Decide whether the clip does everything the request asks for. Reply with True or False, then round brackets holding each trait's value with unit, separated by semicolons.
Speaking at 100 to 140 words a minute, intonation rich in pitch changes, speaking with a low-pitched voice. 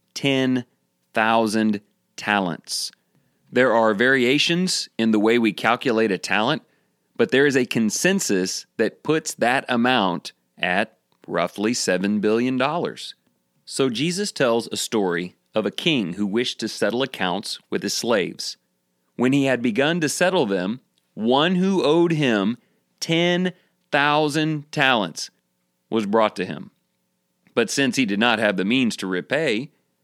True (135 wpm; 6.6 semitones; 120 Hz)